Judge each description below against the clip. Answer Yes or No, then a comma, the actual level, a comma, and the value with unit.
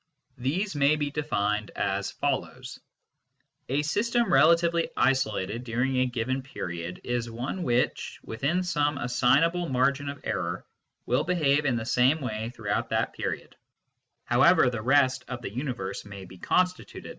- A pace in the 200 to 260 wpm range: No, average, 145 wpm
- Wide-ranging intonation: No, average, 4.4 semitones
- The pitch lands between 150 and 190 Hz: No, low, 130 Hz